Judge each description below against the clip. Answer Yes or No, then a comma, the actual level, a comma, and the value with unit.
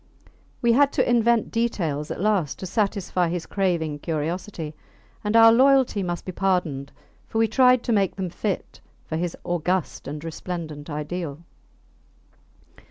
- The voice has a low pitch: No, medium, 180 Hz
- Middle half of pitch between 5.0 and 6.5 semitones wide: Yes, wide, 5.4 semitones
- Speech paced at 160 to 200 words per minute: No, average, 145 wpm